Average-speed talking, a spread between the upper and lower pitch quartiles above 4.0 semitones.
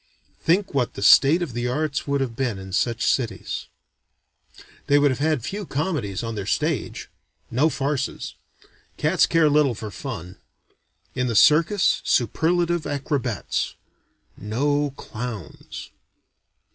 No: slow, 130 wpm; average, 4.8 semitones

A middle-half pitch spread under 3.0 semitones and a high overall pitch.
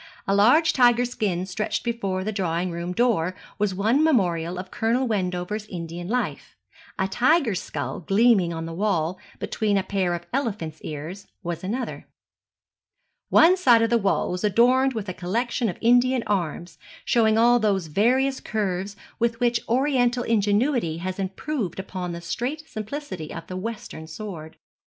No: average, 5.1 semitones; high, 205 Hz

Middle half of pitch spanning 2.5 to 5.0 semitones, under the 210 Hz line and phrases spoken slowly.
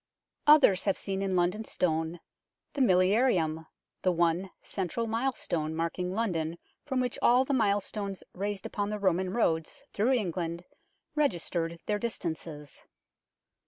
Yes: average, 4.7 semitones; high, 190 Hz; slow, 130 wpm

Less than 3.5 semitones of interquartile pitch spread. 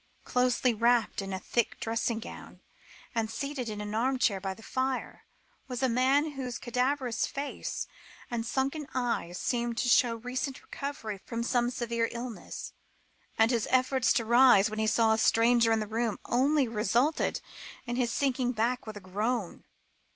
Yes: narrow, 2.4 semitones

